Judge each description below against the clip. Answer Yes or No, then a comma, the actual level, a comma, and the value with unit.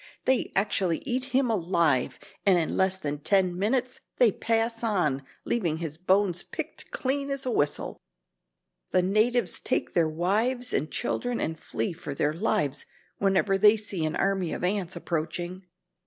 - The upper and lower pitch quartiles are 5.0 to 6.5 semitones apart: Yes, wide, 5.4 semitones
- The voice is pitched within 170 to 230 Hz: Yes, high, 190 Hz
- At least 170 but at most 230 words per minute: No, average, 155 wpm